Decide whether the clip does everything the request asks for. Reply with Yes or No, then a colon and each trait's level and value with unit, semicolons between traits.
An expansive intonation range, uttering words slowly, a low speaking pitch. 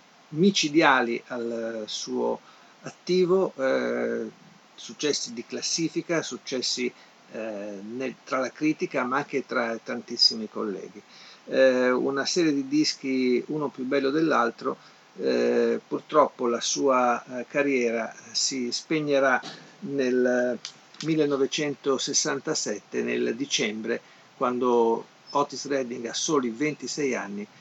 No: average, 4.0 semitones; slow, 100 wpm; low, 130 Hz